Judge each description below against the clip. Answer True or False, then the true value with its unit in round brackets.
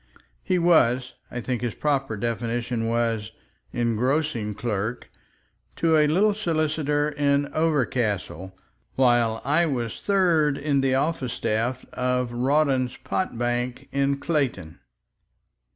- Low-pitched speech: True (130 Hz)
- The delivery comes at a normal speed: False (110 wpm)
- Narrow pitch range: False (4.2 semitones)